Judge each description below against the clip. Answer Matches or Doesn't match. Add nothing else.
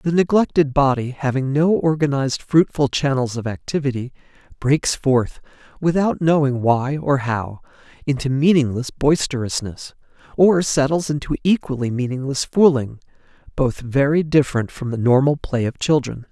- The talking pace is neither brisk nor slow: Doesn't match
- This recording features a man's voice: Matches